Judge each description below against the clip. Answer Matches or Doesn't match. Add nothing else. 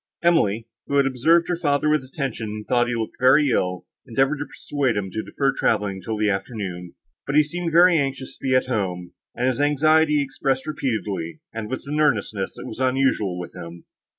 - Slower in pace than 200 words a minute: Doesn't match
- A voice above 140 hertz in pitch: Doesn't match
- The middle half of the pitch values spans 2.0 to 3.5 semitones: Doesn't match